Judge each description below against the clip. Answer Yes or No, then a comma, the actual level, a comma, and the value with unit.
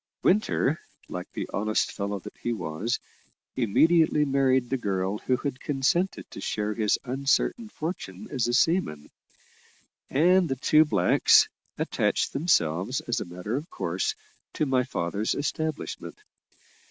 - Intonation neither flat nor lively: No, wide, 6.9 semitones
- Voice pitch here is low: Yes, low, 130 Hz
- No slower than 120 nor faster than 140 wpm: Yes, slow, 135 wpm